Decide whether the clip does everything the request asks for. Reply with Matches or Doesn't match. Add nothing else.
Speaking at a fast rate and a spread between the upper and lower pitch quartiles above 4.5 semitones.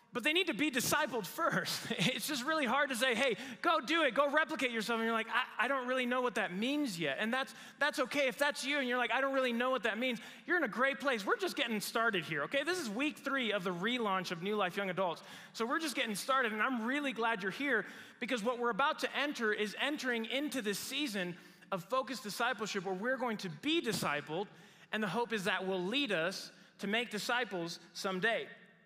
Matches